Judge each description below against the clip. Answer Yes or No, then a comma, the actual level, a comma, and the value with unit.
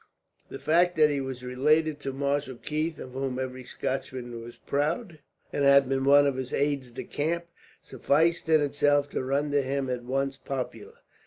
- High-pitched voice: No, medium, 140 Hz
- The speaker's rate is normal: Yes, average, 175 wpm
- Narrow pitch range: Yes, narrow, 2.2 semitones